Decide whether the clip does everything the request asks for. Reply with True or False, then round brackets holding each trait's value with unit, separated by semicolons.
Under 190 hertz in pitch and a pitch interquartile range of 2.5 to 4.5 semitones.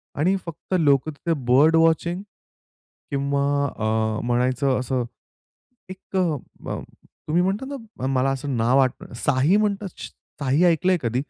False (140 Hz; 5.1 semitones)